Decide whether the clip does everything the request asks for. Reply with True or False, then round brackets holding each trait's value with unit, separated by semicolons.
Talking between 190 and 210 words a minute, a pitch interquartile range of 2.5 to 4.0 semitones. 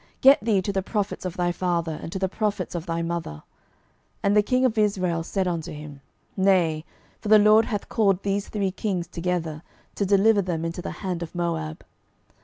True (200 wpm; 3.4 semitones)